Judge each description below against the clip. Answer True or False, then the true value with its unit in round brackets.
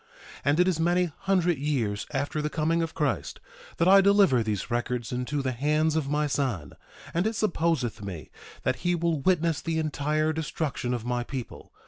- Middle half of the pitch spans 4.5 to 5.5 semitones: True (4.9 semitones)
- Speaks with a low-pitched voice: False (150 Hz)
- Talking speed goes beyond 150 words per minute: True (185 wpm)